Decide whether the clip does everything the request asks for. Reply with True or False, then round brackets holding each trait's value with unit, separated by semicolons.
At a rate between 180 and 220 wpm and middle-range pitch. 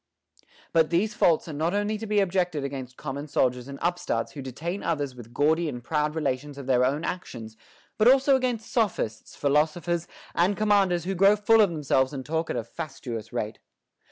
True (185 wpm; 160 Hz)